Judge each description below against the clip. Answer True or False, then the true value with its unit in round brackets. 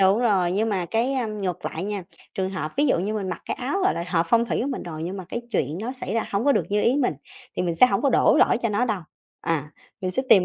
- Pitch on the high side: True (205 Hz)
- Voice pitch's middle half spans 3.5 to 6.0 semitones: True (4.7 semitones)